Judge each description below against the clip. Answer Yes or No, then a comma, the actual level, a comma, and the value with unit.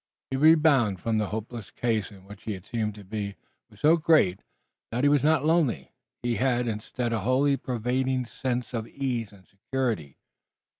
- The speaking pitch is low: Yes, low, 120 Hz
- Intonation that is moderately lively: Yes, average, 3.9 semitones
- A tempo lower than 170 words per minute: No, average, 180 wpm